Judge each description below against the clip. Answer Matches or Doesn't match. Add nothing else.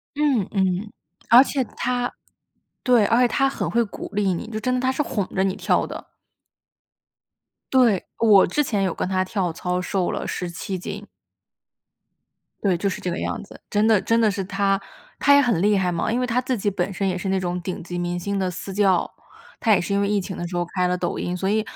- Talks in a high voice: Matches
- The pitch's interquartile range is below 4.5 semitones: Matches